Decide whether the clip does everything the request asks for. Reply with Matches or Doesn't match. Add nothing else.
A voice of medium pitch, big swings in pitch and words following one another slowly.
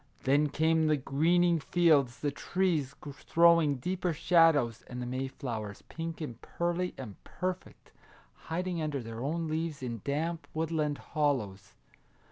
Doesn't match